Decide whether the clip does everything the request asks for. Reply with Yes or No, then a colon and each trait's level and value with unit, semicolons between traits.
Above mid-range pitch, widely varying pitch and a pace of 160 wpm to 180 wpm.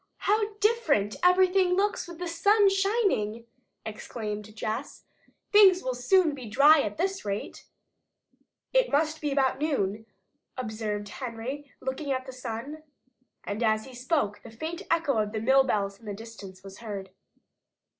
No: very high, 260 Hz; wide, 8.1 semitones; average, 145 wpm